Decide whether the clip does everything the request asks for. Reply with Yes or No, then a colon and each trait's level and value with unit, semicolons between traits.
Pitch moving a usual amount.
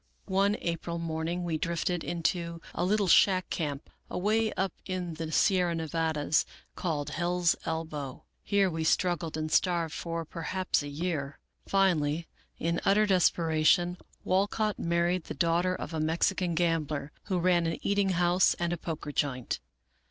No: narrow, 2.3 semitones